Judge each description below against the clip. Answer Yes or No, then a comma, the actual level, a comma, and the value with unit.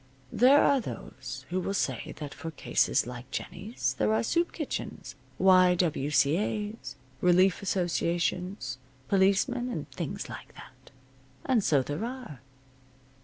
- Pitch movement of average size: No, wide, 7.0 semitones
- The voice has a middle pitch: Yes, medium, 180 Hz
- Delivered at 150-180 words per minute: No, slow, 135 wpm